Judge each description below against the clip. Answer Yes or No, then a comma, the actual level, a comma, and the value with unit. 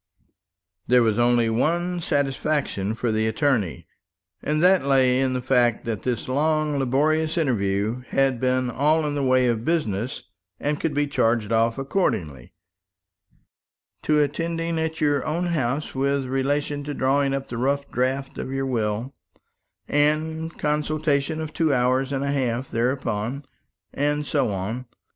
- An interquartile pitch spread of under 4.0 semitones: Yes, average, 3.6 semitones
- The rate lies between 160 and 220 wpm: No, average, 150 wpm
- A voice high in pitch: No, low, 135 Hz